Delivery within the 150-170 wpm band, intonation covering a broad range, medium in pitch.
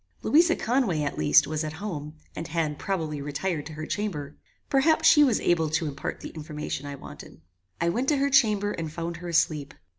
No: average, 200 wpm; wide, 5.7 semitones; medium, 165 Hz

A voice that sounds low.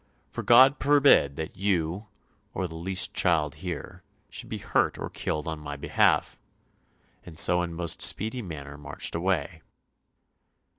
Yes: very low, 85 Hz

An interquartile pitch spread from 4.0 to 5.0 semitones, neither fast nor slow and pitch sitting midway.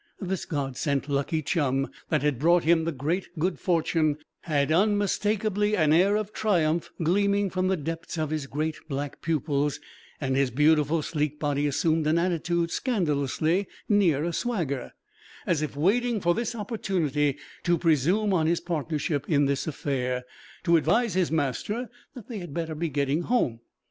Yes: average, 4.3 semitones; average, 165 wpm; medium, 160 Hz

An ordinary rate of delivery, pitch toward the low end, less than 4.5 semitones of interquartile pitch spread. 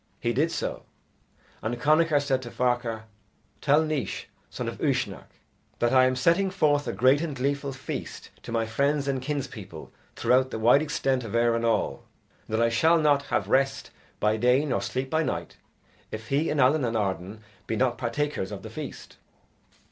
Yes: average, 180 wpm; low, 130 Hz; average, 3.9 semitones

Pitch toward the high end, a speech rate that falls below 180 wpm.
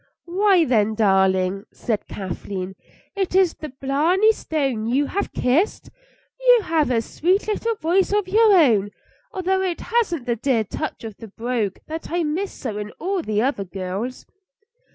Yes: very high, 280 Hz; average, 160 wpm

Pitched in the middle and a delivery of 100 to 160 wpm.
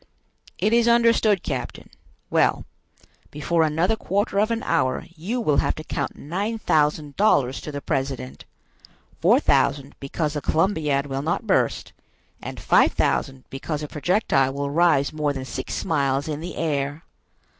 Yes: medium, 150 Hz; average, 155 wpm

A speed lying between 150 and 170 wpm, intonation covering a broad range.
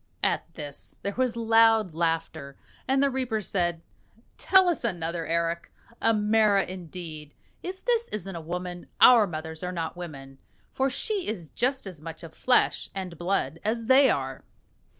Yes: average, 160 wpm; wide, 5.8 semitones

